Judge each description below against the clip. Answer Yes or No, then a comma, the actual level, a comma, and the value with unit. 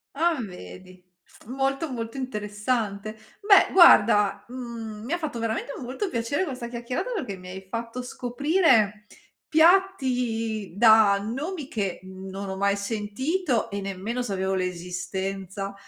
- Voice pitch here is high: Yes, high, 225 Hz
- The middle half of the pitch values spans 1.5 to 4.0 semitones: No, average, 4.9 semitones